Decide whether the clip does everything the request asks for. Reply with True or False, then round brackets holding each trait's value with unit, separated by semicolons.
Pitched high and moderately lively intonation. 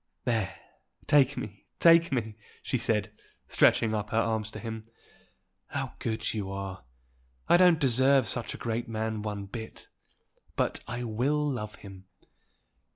False (110 Hz; 3.3 semitones)